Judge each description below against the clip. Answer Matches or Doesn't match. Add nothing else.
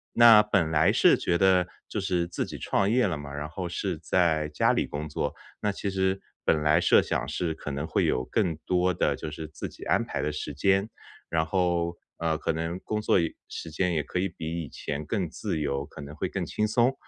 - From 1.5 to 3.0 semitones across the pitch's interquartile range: Doesn't match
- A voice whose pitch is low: Matches